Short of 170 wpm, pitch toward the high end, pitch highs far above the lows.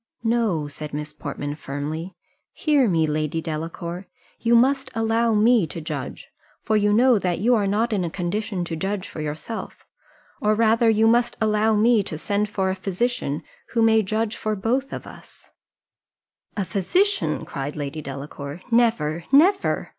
Yes: average, 160 wpm; high, 205 Hz; wide, 6.1 semitones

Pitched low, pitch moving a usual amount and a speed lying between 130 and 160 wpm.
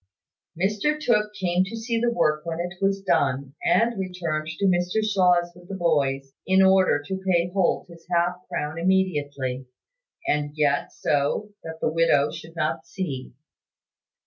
No: medium, 175 Hz; average, 4.0 semitones; average, 155 wpm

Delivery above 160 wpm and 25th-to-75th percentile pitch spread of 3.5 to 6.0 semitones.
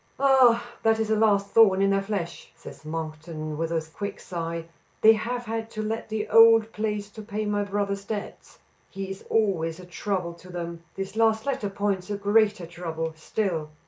Yes: average, 185 wpm; average, 4.3 semitones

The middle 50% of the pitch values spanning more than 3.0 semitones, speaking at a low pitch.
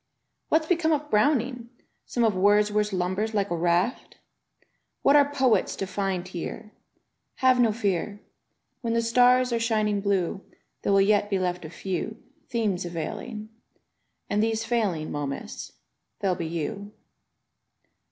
No: average, 3.8 semitones; high, 210 Hz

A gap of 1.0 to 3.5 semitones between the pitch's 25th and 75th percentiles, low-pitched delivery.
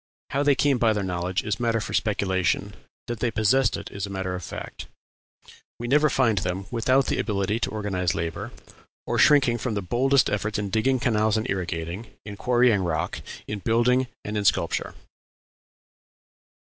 No: average, 4.0 semitones; low, 110 Hz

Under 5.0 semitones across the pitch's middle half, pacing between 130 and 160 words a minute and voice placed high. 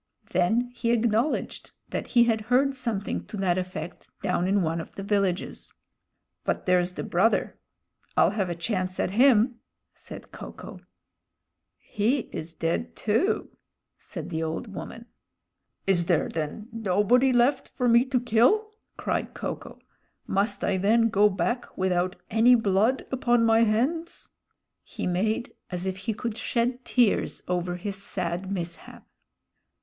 Yes: average, 4.6 semitones; average, 145 wpm; high, 210 Hz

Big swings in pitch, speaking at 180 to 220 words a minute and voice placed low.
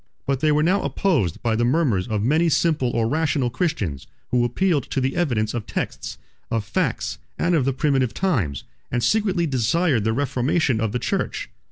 Yes: wide, 6.0 semitones; average, 185 wpm; low, 130 Hz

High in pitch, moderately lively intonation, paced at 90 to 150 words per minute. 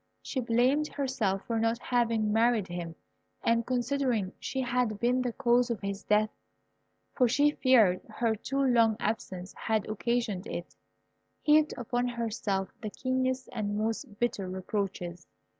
Yes: high, 230 Hz; average, 3.3 semitones; average, 140 wpm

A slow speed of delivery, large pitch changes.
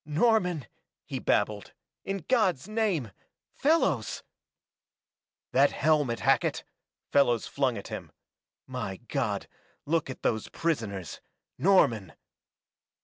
Yes: slow, 100 wpm; wide, 8.1 semitones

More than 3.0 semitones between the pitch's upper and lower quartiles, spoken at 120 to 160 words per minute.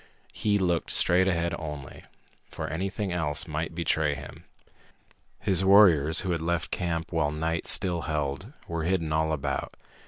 No: average, 2.7 semitones; average, 150 wpm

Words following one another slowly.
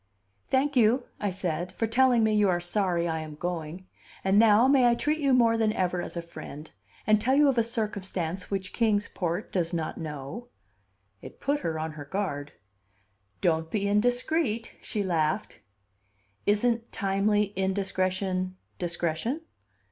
No: average, 155 wpm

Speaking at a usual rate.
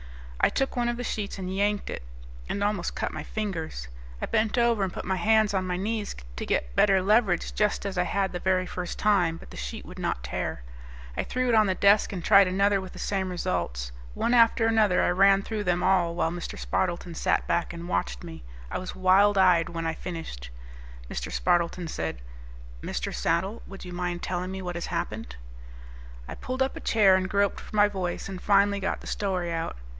No: fast, 210 wpm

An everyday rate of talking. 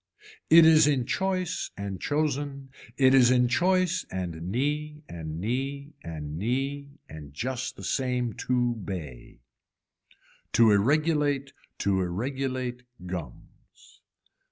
No: slow, 110 wpm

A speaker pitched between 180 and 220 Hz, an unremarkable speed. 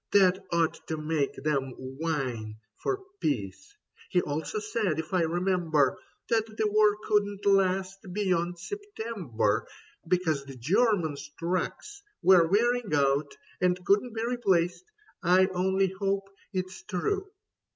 No: medium, 185 Hz; slow, 125 wpm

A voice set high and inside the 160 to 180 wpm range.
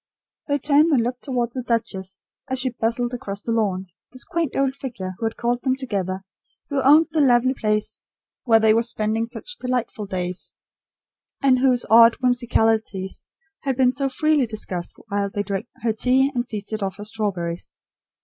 Yes: high, 235 Hz; average, 175 wpm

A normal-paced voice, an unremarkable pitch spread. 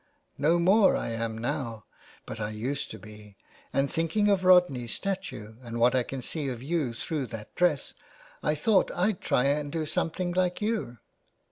No: average, 190 wpm; wide, 7.2 semitones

